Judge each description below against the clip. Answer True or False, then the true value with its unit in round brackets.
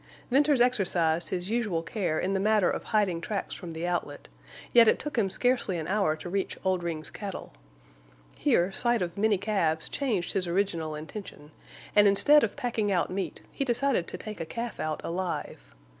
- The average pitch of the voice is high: True (195 Hz)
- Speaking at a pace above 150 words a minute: True (180 wpm)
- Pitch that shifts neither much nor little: True (4.4 semitones)